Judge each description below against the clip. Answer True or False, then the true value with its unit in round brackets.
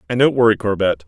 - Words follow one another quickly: True (225 wpm)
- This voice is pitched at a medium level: False (105 Hz)